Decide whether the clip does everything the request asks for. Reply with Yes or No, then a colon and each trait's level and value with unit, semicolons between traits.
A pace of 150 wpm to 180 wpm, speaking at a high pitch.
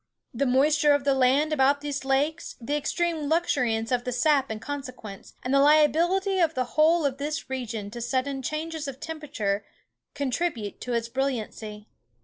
Yes: average, 165 wpm; very high, 275 Hz